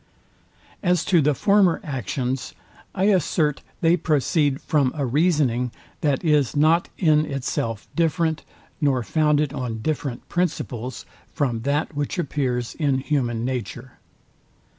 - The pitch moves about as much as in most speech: Yes, average, 3.9 semitones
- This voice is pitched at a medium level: Yes, medium, 145 Hz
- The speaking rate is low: Yes, slow, 120 wpm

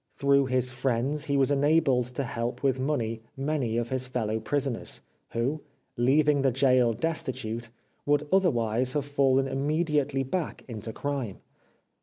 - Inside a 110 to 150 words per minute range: Yes, average, 140 wpm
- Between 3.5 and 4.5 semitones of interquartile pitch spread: No, average, 3.1 semitones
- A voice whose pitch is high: No, low, 135 Hz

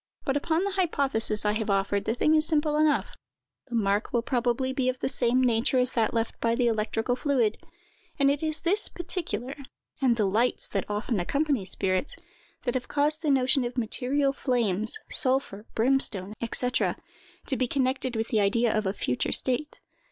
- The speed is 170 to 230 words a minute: Yes, average, 180 wpm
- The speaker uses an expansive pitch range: No, average, 4.3 semitones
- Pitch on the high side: Yes, very high, 250 Hz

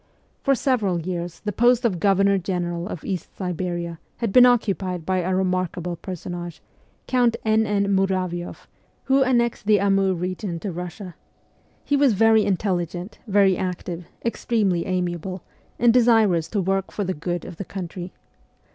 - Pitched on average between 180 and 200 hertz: Yes, high, 190 Hz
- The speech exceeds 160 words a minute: No, average, 150 wpm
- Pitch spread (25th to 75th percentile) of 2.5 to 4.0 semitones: Yes, average, 3.4 semitones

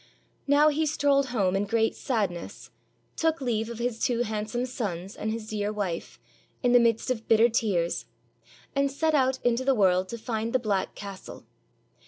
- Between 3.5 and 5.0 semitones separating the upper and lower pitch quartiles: Yes, average, 3.8 semitones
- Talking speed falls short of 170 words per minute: No, average, 175 wpm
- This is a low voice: No, high, 230 Hz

